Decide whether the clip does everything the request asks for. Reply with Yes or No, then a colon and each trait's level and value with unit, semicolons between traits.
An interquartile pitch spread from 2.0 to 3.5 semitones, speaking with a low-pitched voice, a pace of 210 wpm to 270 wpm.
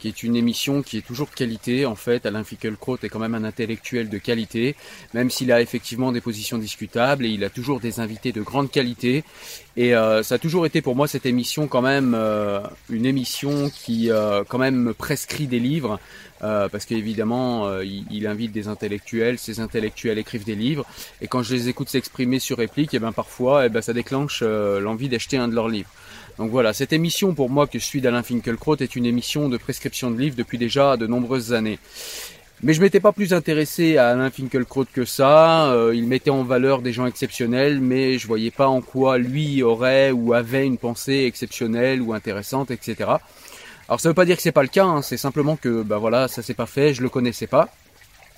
Yes: average, 3.0 semitones; low, 125 Hz; average, 215 wpm